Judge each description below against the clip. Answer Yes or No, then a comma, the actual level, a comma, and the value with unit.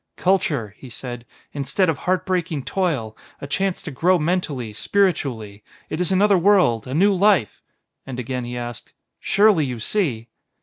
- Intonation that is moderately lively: No, wide, 7.3 semitones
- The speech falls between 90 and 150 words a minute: No, average, 165 wpm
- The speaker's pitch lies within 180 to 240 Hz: No, medium, 150 Hz